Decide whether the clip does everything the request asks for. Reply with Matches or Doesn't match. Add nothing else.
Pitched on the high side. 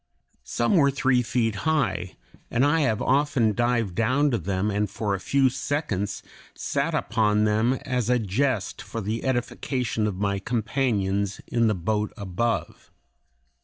Doesn't match